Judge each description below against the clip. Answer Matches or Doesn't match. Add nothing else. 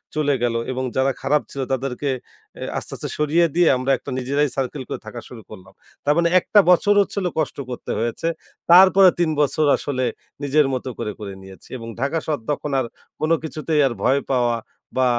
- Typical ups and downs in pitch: Matches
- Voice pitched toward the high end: Doesn't match